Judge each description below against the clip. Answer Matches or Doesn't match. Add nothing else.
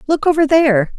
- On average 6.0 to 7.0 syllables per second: Matches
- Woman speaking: Matches